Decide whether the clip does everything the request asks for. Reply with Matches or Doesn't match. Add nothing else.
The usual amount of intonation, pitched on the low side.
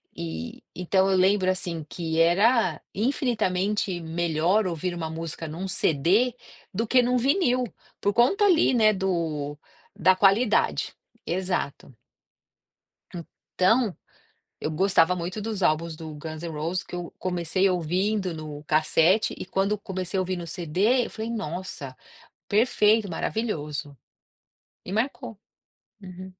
Doesn't match